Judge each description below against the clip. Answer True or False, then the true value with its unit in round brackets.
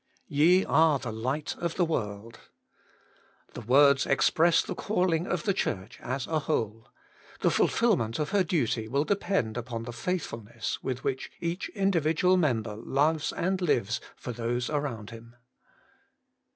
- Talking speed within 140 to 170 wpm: True (150 wpm)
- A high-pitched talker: False (140 Hz)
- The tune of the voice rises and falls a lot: True (6.5 semitones)